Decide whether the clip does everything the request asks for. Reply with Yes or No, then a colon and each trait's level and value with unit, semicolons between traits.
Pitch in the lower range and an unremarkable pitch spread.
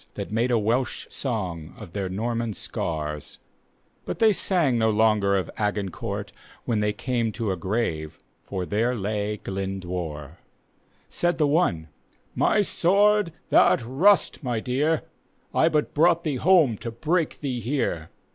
No: low, 115 Hz; wide, 7.3 semitones